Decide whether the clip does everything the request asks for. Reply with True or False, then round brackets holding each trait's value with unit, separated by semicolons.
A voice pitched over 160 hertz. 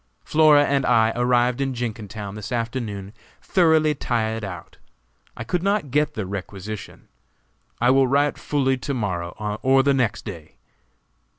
False (120 Hz)